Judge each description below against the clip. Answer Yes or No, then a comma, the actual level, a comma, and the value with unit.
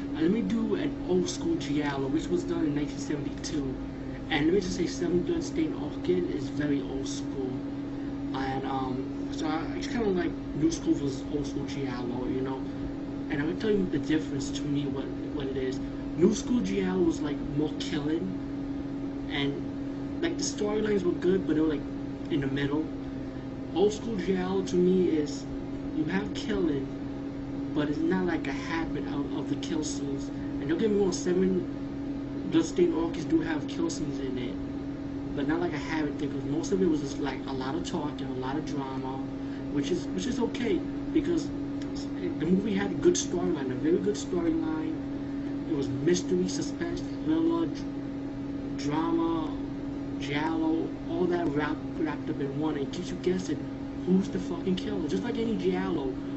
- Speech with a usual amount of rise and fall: No, wide, 8.3 semitones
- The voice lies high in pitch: No, medium, 140 Hz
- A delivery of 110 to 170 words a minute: No, average, 185 wpm